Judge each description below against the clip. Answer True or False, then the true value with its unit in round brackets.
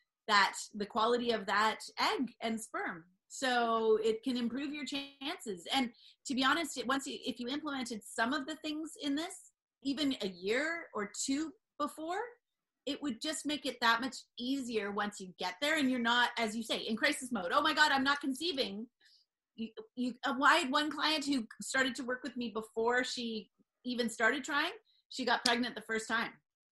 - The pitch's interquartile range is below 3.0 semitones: False (4.3 semitones)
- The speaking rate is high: False (190 wpm)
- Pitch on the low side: False (255 Hz)